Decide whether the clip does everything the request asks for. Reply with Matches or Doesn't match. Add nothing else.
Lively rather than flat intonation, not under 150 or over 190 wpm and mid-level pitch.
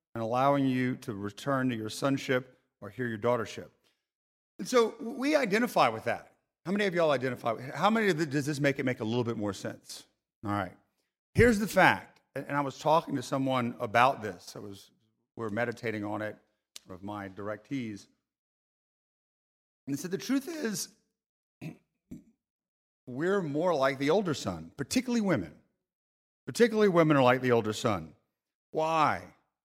Doesn't match